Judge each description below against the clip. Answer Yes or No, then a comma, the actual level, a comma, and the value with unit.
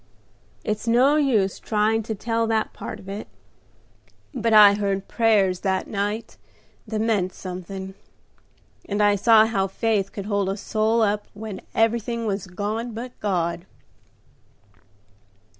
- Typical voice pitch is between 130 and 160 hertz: No, high, 210 Hz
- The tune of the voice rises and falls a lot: No, narrow, 2.5 semitones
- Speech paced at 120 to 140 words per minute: Yes, slow, 135 wpm